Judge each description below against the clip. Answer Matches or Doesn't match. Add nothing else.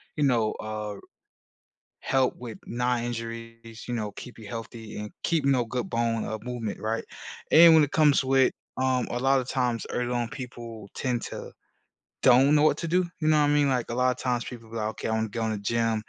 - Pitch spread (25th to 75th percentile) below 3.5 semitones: Matches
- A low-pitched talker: Matches